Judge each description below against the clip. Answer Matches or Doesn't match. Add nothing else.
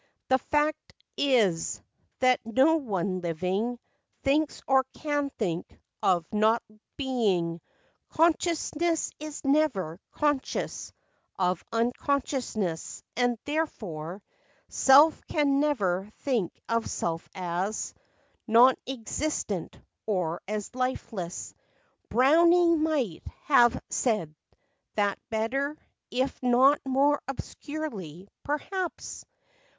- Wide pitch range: Matches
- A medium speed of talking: Doesn't match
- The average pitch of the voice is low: Doesn't match